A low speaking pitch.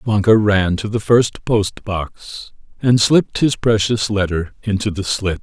Yes: low, 105 Hz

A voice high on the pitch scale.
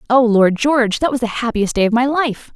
Yes: high, 240 Hz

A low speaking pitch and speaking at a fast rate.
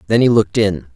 Yes: low, 110 Hz; fast, 250 wpm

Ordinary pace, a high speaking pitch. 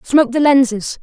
Yes: average, 175 wpm; very high, 260 Hz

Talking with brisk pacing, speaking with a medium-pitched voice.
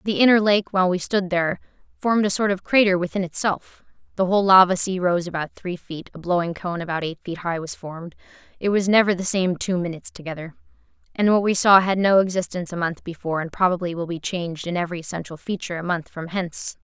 Yes: fast, 220 wpm; medium, 180 Hz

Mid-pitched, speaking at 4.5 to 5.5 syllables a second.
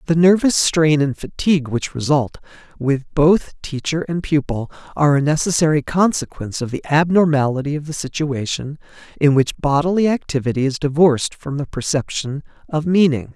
Yes: medium, 150 Hz; 5.3 syllables/s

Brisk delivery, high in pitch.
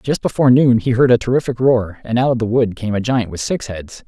No: fast, 280 wpm; low, 120 Hz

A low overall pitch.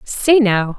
No: high, 220 Hz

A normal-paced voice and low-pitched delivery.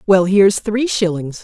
No: average, 165 wpm; high, 195 Hz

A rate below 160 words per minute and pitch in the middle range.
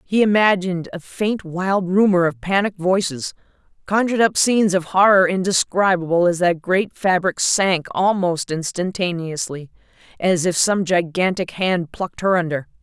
Yes: average, 140 wpm; medium, 180 Hz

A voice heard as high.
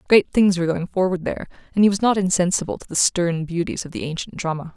No: medium, 180 Hz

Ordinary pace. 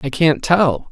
Yes: average, 195 wpm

